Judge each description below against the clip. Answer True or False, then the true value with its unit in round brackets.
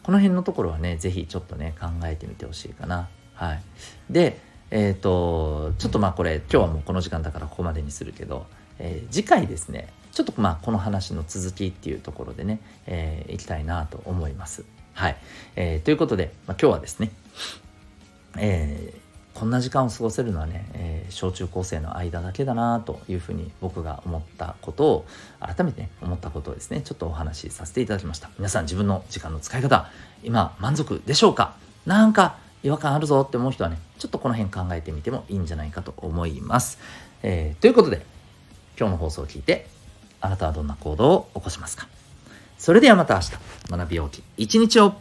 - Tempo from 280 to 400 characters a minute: True (385 characters per minute)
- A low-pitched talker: True (90 Hz)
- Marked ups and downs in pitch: False (4.7 semitones)